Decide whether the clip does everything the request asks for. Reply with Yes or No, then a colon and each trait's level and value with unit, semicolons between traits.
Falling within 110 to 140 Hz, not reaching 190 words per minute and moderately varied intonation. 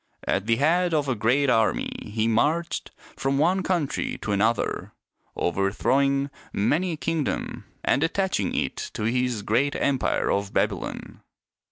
No: low, 135 Hz; average, 140 wpm; wide, 6.1 semitones